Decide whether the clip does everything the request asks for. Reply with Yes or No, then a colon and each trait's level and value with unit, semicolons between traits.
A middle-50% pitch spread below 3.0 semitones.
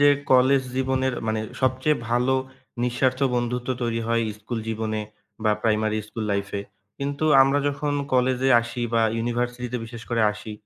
Yes: narrow, 2.6 semitones